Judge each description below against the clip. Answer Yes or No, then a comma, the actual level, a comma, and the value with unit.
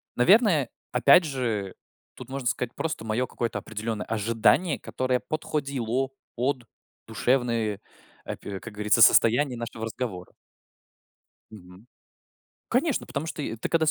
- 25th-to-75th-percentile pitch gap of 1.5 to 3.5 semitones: No, average, 4.0 semitones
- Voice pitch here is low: Yes, low, 120 Hz